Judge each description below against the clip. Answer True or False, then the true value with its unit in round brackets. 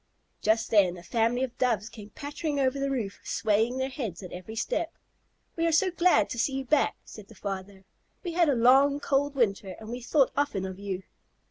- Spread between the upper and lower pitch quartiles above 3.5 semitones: True (5.6 semitones)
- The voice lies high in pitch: True (240 Hz)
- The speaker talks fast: True (210 wpm)